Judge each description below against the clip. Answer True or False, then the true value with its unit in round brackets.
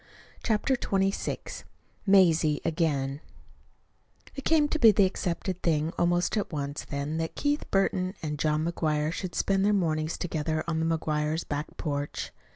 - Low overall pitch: False (165 Hz)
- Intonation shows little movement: False (4.0 semitones)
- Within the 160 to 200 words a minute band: False (150 wpm)